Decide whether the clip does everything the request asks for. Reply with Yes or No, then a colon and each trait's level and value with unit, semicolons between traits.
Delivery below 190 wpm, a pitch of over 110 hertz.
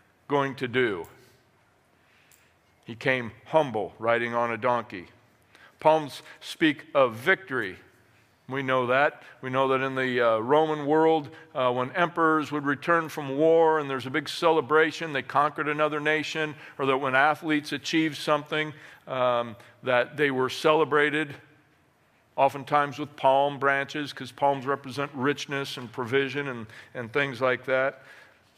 Yes: average, 140 wpm; medium, 140 Hz